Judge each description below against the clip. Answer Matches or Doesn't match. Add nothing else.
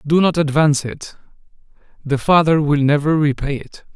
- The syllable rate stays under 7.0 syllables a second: Matches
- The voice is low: Doesn't match